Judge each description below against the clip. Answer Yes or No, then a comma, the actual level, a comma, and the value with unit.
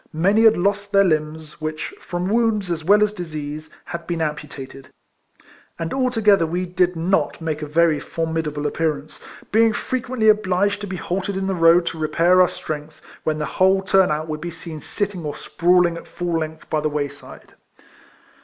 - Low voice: No, medium, 170 Hz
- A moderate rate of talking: Yes, average, 180 wpm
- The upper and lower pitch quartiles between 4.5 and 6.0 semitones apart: No, average, 3.8 semitones